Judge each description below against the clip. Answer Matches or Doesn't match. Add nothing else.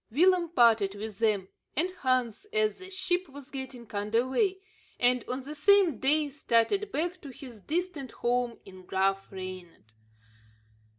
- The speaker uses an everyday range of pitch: Doesn't match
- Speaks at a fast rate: Doesn't match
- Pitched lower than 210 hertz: Doesn't match